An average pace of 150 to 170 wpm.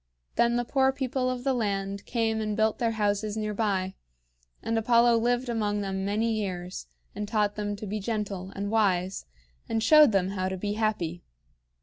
No: average, 185 wpm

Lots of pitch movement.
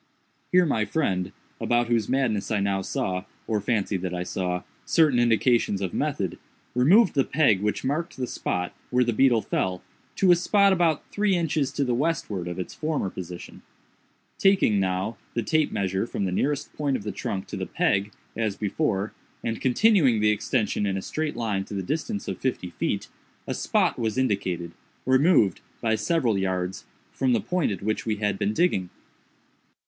Yes: wide, 6.6 semitones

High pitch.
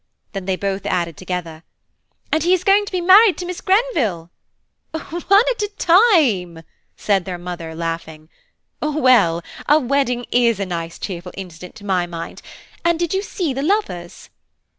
Yes: high, 215 Hz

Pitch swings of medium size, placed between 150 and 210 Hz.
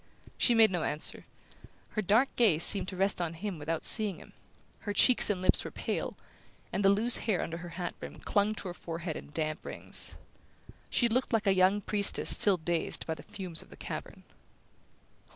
Yes: average, 3.9 semitones; high, 190 Hz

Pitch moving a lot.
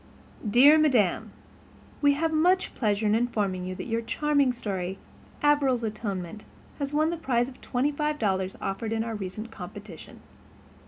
Yes: wide, 5.9 semitones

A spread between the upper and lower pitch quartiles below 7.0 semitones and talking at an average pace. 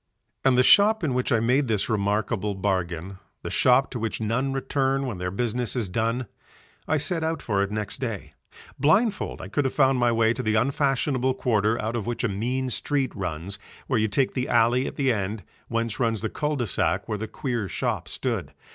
No: average, 3.9 semitones; fast, 210 wpm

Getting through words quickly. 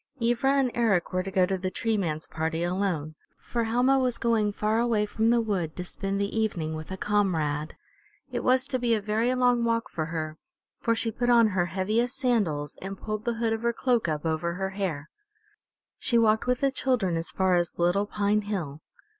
Yes: fast, 210 wpm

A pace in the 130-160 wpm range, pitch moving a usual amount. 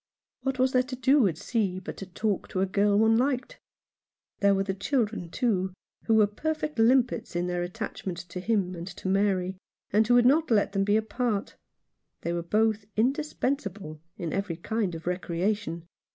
No: average, 180 wpm; average, 4.5 semitones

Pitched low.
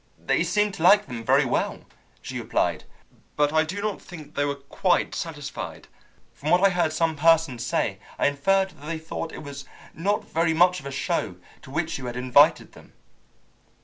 No: medium, 160 Hz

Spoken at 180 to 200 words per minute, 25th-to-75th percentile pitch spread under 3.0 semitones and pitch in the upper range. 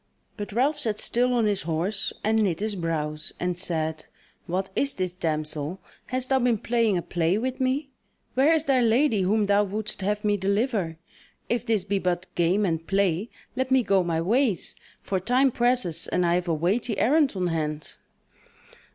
No: average, 185 wpm; wide, 5.6 semitones; high, 200 Hz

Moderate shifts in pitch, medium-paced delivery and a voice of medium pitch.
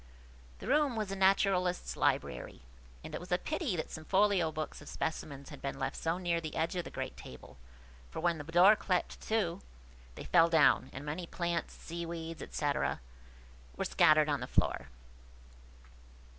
Yes: average, 3.2 semitones; average, 175 wpm; medium, 170 Hz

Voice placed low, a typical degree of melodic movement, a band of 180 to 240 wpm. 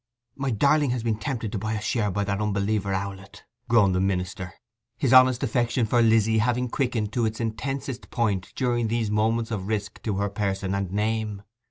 Yes: low, 110 Hz; average, 3.0 semitones; average, 190 wpm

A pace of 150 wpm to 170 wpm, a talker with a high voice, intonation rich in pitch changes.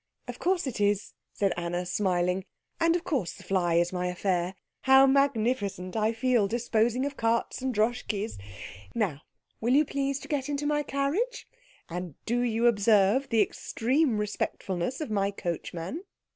Yes: average, 160 wpm; high, 225 Hz; wide, 6.1 semitones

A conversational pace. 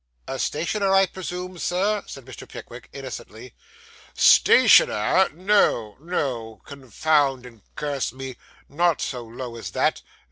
No: slow, 120 wpm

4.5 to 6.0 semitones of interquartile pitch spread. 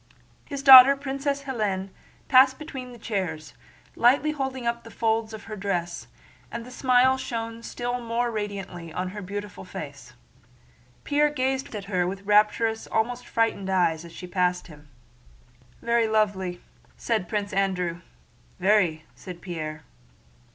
Yes: average, 5.3 semitones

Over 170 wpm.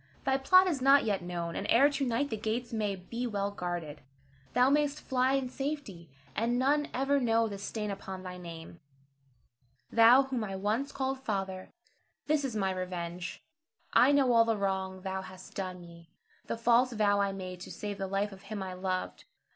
Yes: average, 190 wpm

